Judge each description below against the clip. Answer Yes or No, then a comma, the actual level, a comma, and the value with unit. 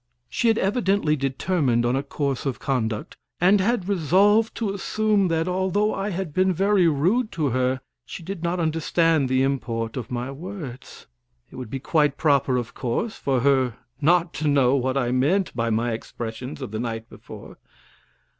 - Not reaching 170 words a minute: No, average, 175 wpm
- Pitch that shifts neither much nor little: No, wide, 6.6 semitones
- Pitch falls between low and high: Yes, medium, 145 Hz